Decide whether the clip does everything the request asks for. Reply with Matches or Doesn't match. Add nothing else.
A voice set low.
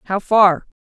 Doesn't match